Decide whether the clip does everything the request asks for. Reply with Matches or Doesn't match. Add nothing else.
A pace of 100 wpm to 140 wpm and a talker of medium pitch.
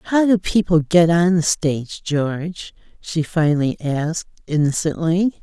Matches